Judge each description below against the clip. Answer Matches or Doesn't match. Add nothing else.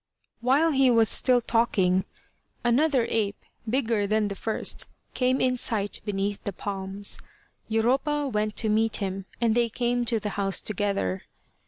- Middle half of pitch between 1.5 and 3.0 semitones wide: Doesn't match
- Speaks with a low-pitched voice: Doesn't match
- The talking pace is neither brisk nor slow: Matches